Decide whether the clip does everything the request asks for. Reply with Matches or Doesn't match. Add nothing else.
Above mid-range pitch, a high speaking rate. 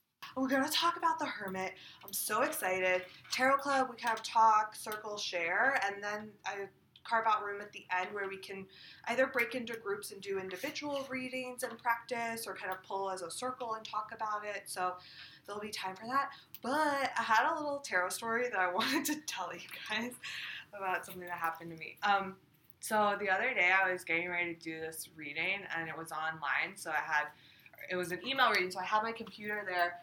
Matches